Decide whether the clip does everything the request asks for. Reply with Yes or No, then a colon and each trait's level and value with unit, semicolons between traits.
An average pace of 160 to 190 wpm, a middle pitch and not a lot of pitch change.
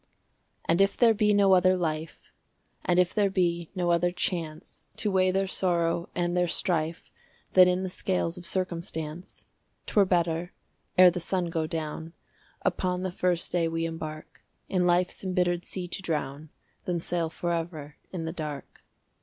Yes: average, 165 wpm; medium, 175 Hz; narrow, 2.0 semitones